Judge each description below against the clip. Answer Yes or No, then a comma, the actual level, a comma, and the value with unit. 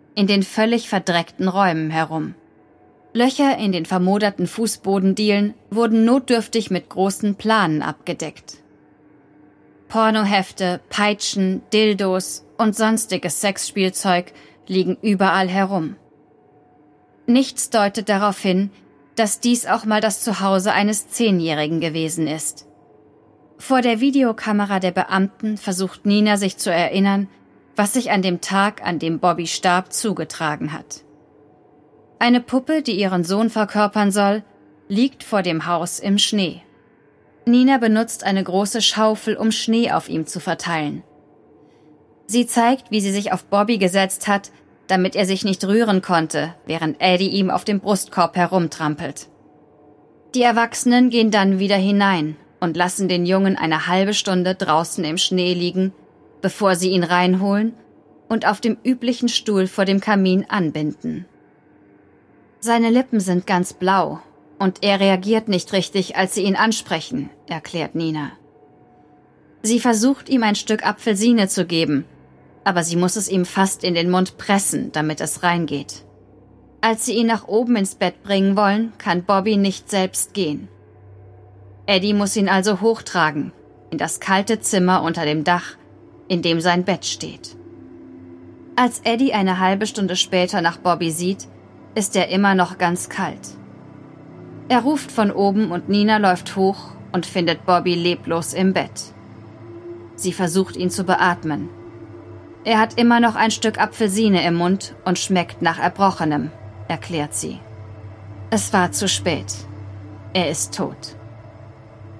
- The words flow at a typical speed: Yes, average, 140 wpm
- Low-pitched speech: No, high, 190 Hz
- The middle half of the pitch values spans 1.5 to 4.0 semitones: No, average, 4.7 semitones